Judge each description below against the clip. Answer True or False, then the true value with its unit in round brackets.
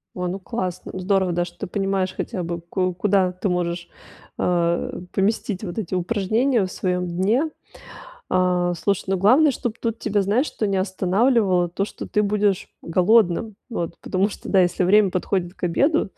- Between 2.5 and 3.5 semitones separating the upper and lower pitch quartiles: True (2.8 semitones)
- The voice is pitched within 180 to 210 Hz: True (190 Hz)